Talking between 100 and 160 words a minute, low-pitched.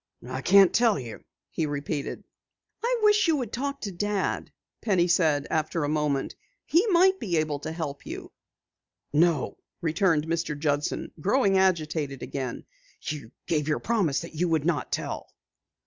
No: average, 155 wpm; medium, 165 Hz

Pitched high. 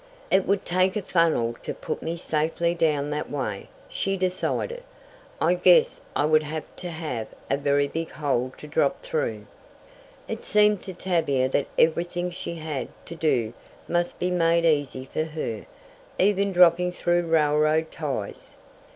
No: medium, 165 Hz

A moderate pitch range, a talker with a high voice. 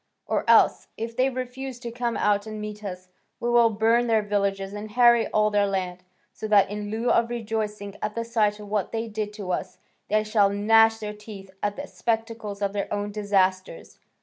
No: narrow, 2.0 semitones; high, 210 Hz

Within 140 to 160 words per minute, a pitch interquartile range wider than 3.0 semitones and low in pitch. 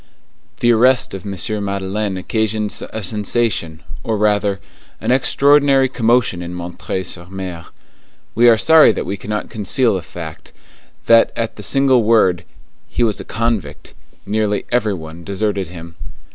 Yes: average, 145 wpm; average, 3.7 semitones; low, 105 Hz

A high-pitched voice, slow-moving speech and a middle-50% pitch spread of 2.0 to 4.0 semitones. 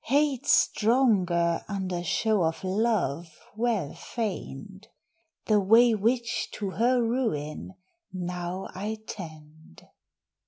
No: high, 195 Hz; slow, 95 wpm; average, 4.9 semitones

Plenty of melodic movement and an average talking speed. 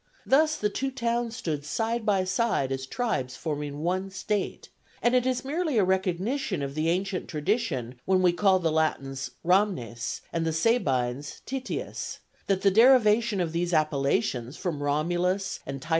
Yes: wide, 7.2 semitones; average, 160 wpm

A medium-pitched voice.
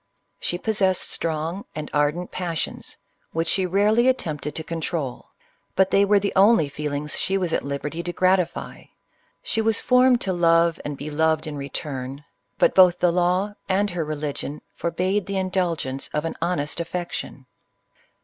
Yes: medium, 170 Hz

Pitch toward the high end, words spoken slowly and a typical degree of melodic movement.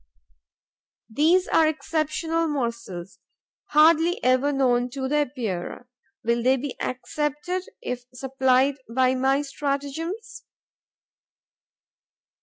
Yes: very high, 275 Hz; slow, 90 wpm; average, 3.5 semitones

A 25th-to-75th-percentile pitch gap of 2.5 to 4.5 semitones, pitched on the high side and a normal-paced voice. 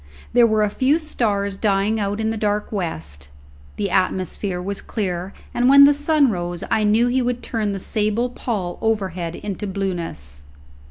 Yes: average, 3.8 semitones; high, 205 Hz; average, 170 wpm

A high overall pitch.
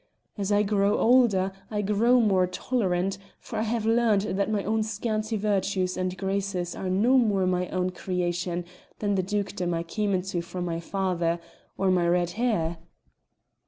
Yes: high, 195 Hz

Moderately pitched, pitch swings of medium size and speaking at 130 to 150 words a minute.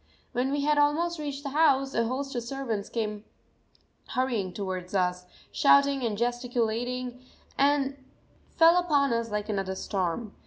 No: very high, 250 Hz; average, 4.9 semitones; average, 145 wpm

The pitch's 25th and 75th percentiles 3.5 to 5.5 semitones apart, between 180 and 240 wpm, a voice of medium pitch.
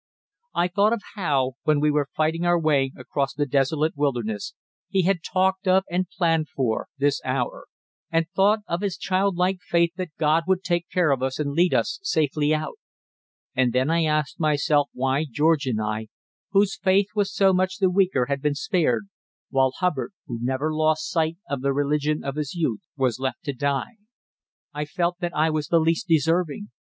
Yes: average, 4.3 semitones; average, 185 wpm; medium, 155 Hz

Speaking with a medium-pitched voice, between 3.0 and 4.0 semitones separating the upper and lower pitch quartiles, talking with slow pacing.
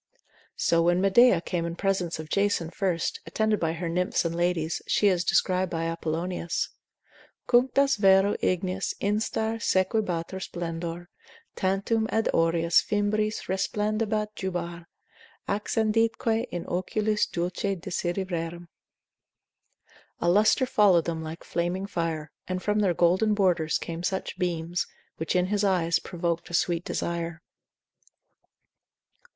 Yes: medium, 180 Hz; average, 3.4 semitones; slow, 125 wpm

